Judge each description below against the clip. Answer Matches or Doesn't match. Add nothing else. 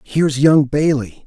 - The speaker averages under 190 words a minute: Matches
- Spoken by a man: Matches